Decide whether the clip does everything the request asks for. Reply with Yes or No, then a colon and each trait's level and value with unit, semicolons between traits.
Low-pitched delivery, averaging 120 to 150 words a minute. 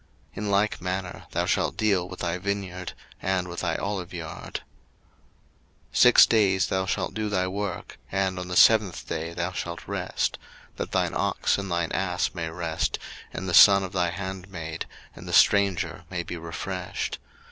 No: very low, 90 Hz; average, 170 wpm